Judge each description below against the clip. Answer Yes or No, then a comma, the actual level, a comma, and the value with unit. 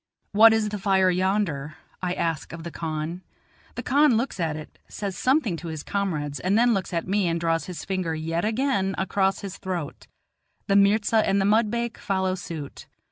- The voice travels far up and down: No, average, 3.8 semitones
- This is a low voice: No, high, 190 Hz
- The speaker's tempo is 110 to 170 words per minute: No, average, 190 wpm